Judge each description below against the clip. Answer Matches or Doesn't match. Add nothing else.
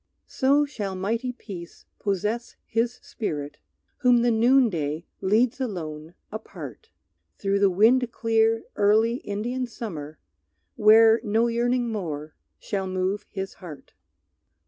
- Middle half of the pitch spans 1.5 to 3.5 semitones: Doesn't match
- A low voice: Doesn't match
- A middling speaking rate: Doesn't match